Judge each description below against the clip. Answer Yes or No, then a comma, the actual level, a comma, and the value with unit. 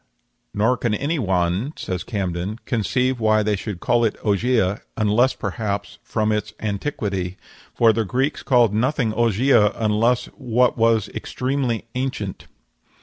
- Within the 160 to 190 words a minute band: No, slow, 135 wpm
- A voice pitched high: No, low, 110 Hz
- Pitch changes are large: No, average, 3.3 semitones